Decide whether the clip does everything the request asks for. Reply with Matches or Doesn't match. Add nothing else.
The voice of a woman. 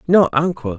Doesn't match